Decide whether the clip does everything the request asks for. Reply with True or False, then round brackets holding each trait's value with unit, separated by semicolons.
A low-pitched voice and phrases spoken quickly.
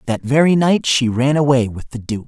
True (130 Hz; 235 wpm)